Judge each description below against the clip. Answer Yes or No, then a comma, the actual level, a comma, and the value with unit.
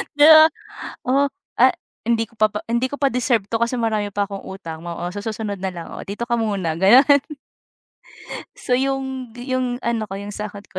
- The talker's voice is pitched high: Yes, high, 225 Hz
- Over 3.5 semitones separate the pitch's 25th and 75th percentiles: Yes, average, 4.0 semitones